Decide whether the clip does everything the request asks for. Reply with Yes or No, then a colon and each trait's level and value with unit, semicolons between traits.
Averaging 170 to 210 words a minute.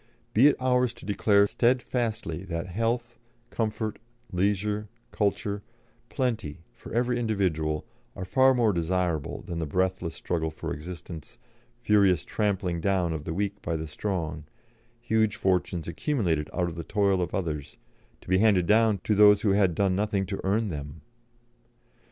No: average, 150 wpm